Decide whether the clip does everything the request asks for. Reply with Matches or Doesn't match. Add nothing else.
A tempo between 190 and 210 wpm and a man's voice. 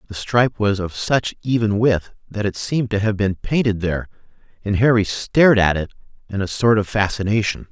Matches